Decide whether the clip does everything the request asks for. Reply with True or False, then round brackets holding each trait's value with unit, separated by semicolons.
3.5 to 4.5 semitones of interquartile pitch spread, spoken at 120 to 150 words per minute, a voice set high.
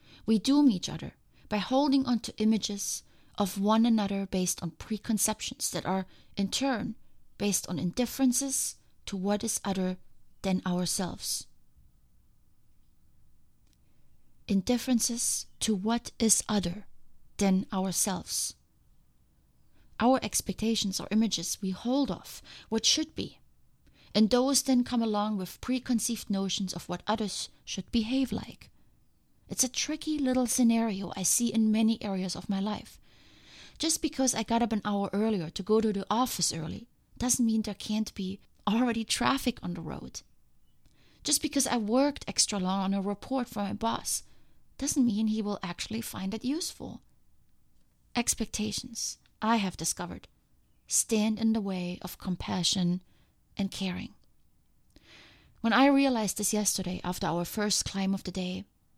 True (3.8 semitones; 140 wpm; 210 Hz)